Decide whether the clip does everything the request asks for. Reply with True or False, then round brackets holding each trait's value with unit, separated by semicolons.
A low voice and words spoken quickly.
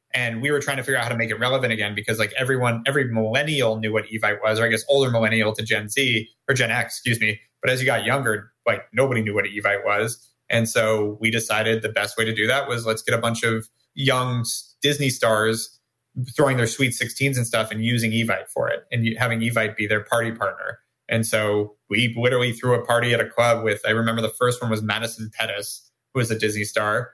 True (115 Hz; 235 wpm)